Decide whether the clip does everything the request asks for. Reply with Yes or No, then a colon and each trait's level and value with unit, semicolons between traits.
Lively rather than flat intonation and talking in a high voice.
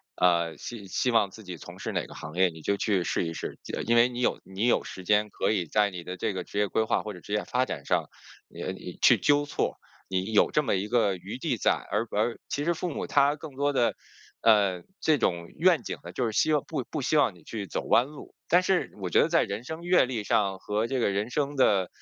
No: wide, 6.1 semitones; low, 110 Hz